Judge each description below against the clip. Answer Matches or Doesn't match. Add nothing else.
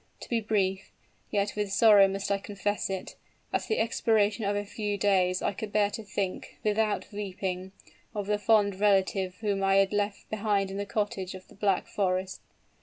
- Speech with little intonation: Matches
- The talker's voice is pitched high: Matches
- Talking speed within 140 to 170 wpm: Doesn't match